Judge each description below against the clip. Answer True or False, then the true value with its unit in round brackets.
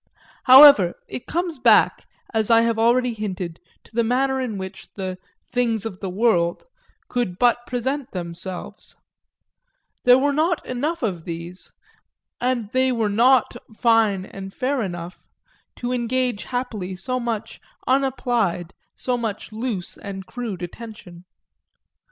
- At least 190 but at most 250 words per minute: False (135 wpm)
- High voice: True (230 Hz)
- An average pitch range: True (4.8 semitones)